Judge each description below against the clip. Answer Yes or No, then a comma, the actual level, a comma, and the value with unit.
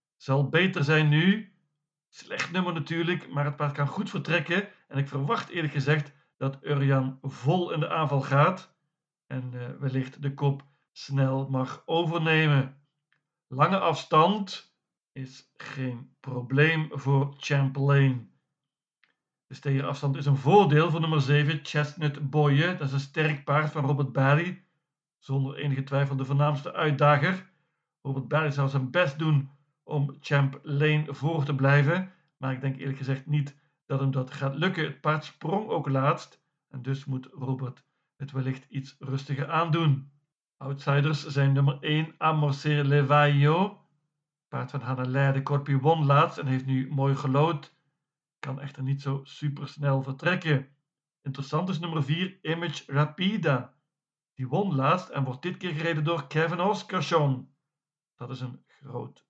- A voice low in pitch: No, medium, 145 Hz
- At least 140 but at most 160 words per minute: Yes, average, 150 wpm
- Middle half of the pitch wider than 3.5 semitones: No, narrow, 2.4 semitones